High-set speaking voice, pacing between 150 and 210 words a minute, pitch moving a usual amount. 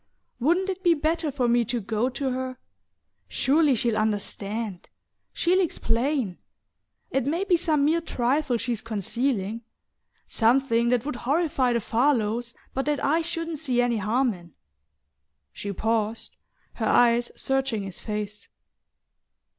No: high, 245 Hz; slow, 135 wpm; average, 4.6 semitones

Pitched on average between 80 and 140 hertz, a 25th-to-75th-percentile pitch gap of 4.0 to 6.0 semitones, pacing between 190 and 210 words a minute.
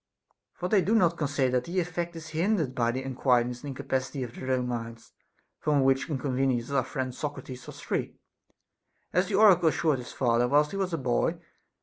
Yes: low, 135 Hz; average, 4.8 semitones; average, 200 wpm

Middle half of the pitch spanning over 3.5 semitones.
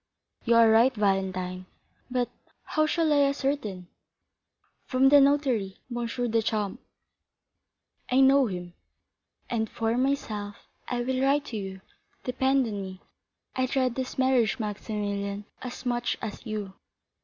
Yes: average, 4.4 semitones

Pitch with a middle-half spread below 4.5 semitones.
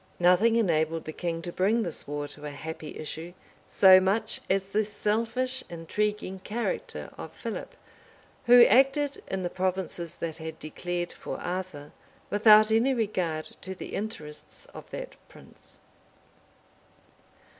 No: average, 4.9 semitones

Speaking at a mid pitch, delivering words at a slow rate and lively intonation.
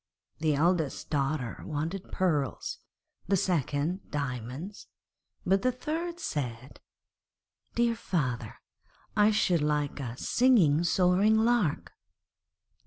Yes: medium, 165 Hz; slow, 95 wpm; wide, 6.2 semitones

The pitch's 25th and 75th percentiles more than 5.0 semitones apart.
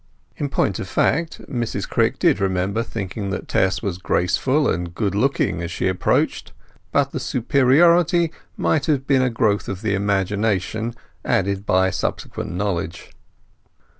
Yes: wide, 5.6 semitones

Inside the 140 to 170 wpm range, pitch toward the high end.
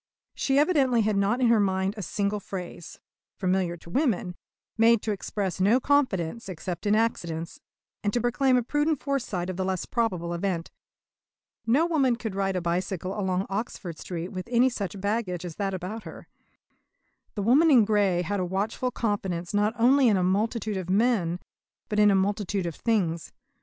No: average, 180 wpm; high, 200 Hz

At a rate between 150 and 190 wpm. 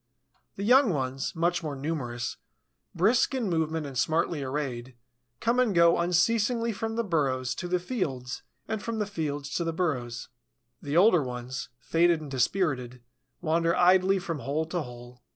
Yes: average, 160 wpm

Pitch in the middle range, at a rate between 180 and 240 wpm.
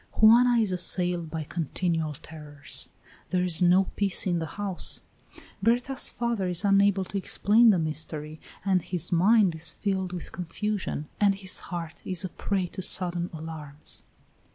No: medium, 180 Hz; average, 155 wpm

